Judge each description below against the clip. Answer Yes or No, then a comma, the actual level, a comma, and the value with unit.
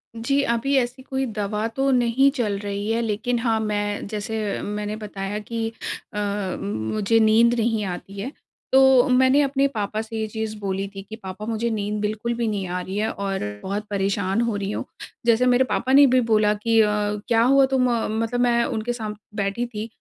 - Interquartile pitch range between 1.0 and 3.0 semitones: Yes, narrow, 2.6 semitones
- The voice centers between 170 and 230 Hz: Yes, high, 220 Hz